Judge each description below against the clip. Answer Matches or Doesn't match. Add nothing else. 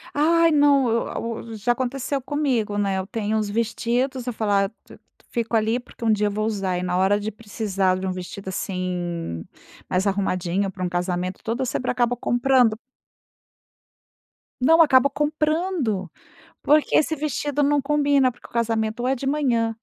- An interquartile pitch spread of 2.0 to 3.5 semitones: Doesn't match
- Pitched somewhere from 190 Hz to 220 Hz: Doesn't match